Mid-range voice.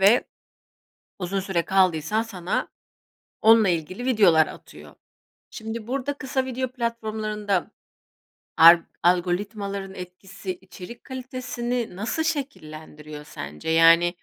No: high, 200 Hz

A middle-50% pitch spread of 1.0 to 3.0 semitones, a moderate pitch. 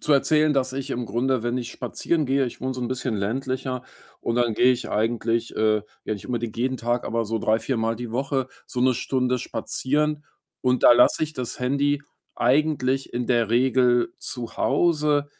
No: narrow, 2.4 semitones; low, 125 Hz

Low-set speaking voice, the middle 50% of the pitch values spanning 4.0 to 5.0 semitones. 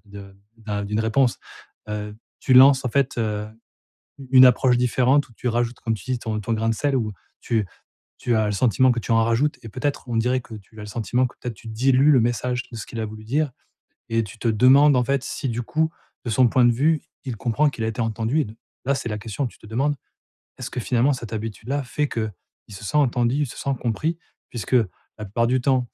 No: low, 120 Hz; average, 2.8 semitones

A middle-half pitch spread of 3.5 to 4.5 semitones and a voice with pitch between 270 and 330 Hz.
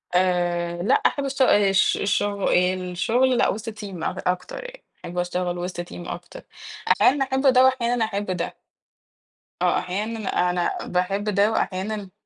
No: average, 4.2 semitones; high, 200 Hz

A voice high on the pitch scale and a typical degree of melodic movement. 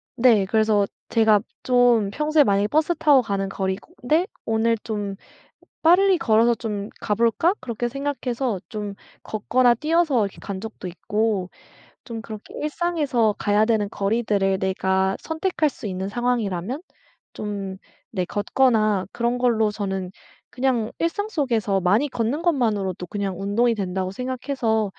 Yes: high, 220 Hz; average, 4.1 semitones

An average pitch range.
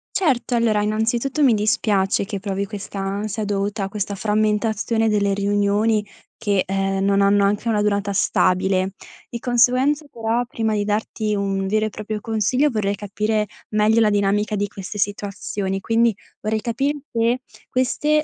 No: narrow, 2.2 semitones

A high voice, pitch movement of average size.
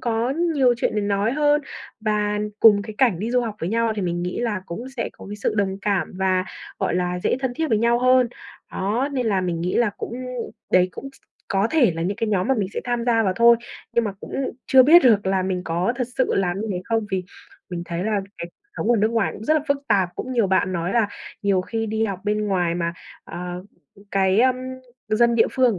Yes: high, 210 Hz; average, 4.0 semitones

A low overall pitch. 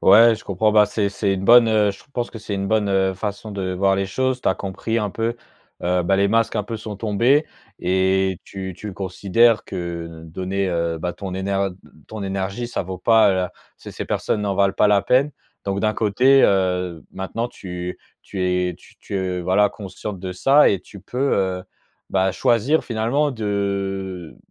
Yes: low, 100 Hz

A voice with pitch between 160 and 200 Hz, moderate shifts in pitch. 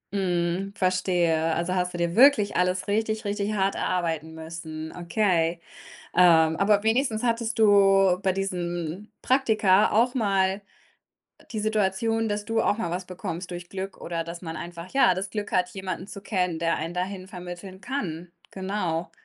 Yes: medium, 185 Hz; average, 3.1 semitones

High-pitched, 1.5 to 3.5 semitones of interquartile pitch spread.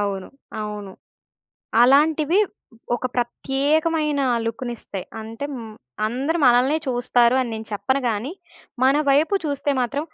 No: very high, 255 Hz; average, 4.1 semitones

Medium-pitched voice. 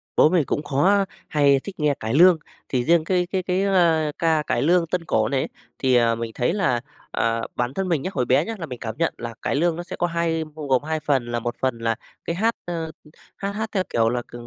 Yes: medium, 155 Hz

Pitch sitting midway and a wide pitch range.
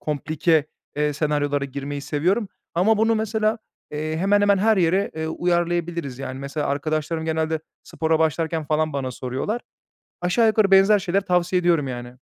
No: medium, 160 Hz; average, 4.6 semitones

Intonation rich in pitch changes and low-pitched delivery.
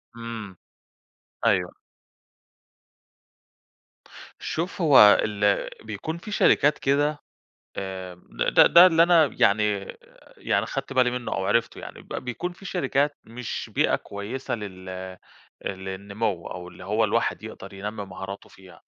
Yes: wide, 6.5 semitones; low, 110 Hz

